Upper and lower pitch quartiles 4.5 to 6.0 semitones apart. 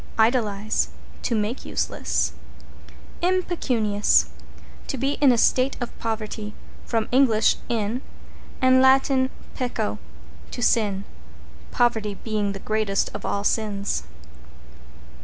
No: average, 3.5 semitones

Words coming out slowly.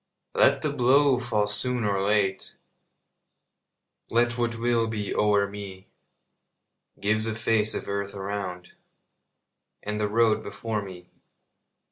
Yes: slow, 120 wpm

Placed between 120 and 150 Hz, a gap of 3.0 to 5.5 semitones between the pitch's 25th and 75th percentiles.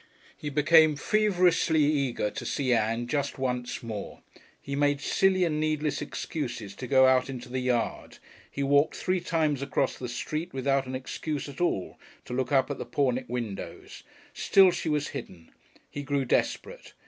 Yes: medium, 140 Hz; average, 3.3 semitones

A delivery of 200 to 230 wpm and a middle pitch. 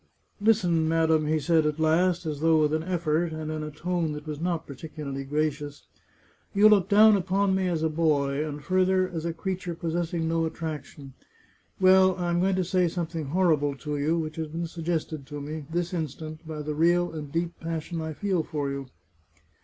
Yes: fast, 205 wpm; medium, 160 Hz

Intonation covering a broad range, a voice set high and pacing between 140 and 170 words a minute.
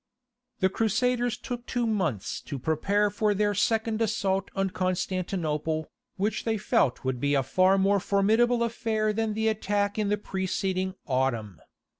No: average, 3.1 semitones; high, 200 Hz; average, 150 wpm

